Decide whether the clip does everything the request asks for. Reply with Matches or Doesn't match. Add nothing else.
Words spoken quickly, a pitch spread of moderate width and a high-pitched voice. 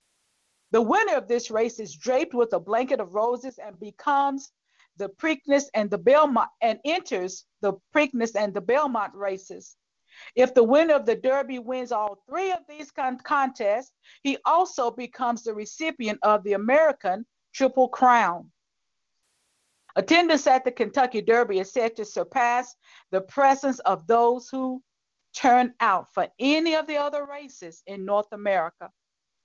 Doesn't match